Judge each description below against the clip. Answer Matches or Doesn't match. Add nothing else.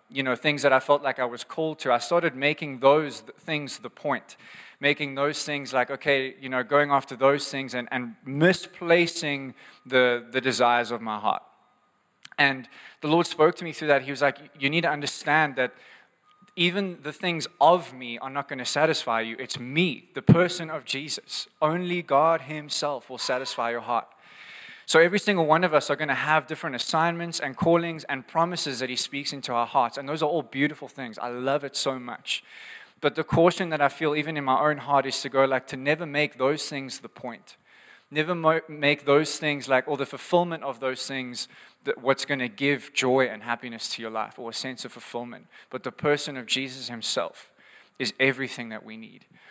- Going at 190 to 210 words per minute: Matches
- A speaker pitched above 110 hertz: Matches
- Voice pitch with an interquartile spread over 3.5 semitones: Doesn't match